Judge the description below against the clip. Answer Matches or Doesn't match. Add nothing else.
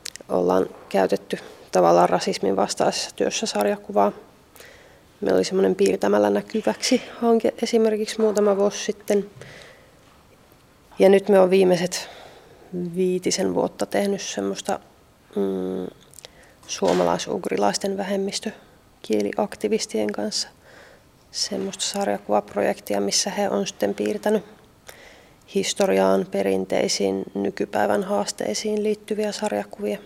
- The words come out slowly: Matches